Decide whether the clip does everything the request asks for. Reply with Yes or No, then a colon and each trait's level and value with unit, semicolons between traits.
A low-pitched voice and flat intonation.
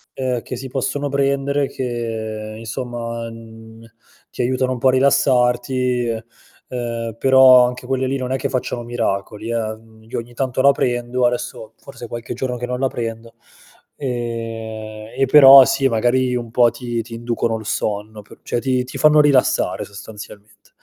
Yes: low, 120 Hz; narrow, 2.3 semitones